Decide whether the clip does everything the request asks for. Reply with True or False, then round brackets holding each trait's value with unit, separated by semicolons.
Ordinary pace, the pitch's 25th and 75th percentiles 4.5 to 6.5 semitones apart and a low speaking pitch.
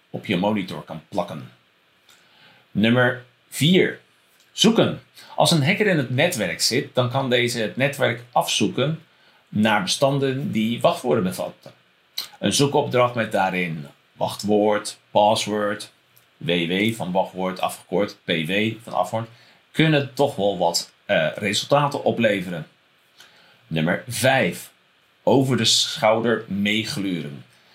False (110 wpm; 5.3 semitones; 110 Hz)